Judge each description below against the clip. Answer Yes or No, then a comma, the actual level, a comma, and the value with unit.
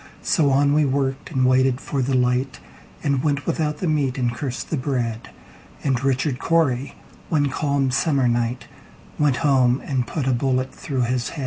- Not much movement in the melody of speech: Yes, narrow, 2.3 semitones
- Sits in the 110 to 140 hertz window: Yes, low, 135 Hz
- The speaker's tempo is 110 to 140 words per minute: No, average, 160 wpm